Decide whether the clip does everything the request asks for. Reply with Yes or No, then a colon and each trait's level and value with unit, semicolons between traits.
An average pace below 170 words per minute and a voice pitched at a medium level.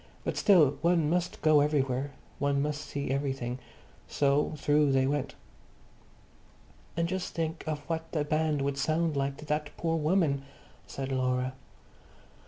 Yes: average, 145 wpm; medium, 145 Hz